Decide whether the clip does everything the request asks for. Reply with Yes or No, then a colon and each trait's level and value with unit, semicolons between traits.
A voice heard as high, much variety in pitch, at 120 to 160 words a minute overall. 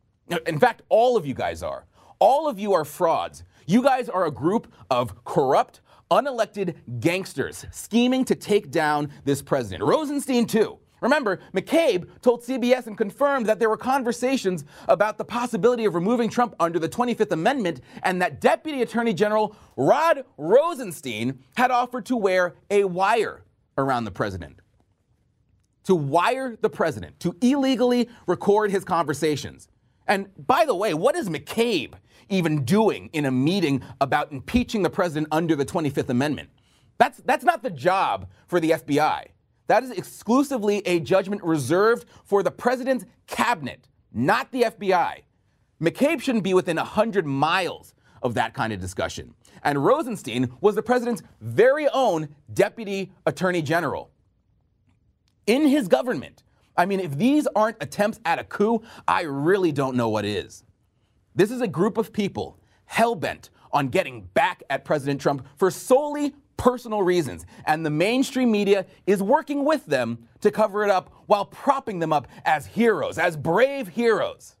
Yes: high, 195 Hz; wide, 7.7 semitones; average, 155 wpm